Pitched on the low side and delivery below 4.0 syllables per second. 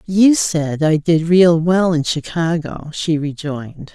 No: medium, 165 Hz; 3.7 syllables/s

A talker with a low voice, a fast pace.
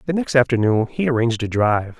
Yes: low, 125 Hz; fast, 210 wpm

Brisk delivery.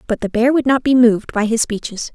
Yes: fast, 280 wpm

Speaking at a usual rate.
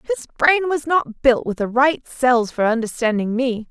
Yes: average, 195 wpm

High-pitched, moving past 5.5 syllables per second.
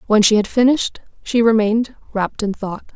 Yes: high, 220 Hz; 6.0 syllables/s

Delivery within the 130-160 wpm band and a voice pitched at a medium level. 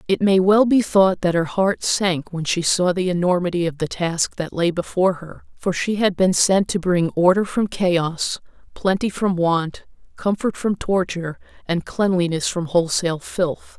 No: average, 185 wpm; medium, 180 Hz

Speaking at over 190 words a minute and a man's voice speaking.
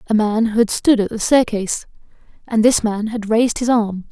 No: fast, 205 wpm; female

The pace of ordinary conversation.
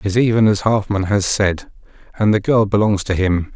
No: fast, 220 wpm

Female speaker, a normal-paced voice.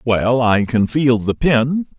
No: male; average, 180 wpm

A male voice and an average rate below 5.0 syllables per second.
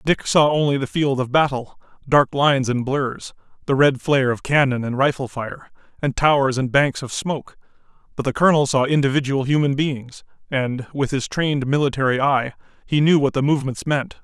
No: male; 5.4 syllables/s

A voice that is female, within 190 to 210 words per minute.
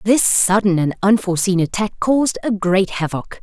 No: female; average, 160 wpm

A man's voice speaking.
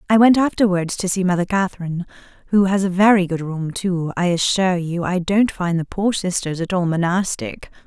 No: female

